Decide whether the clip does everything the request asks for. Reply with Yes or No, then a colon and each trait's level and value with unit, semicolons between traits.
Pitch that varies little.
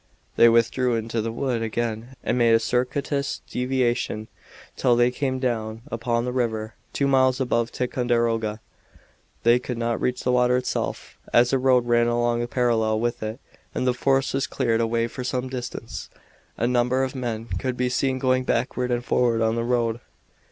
Yes: narrow, 1.6 semitones